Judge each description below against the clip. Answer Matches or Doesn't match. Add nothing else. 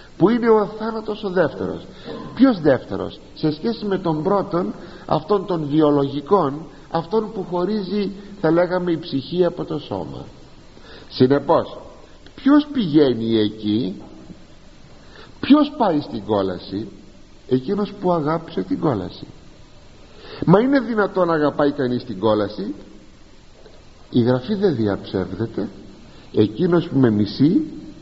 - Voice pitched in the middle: Matches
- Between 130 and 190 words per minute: Doesn't match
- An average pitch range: Doesn't match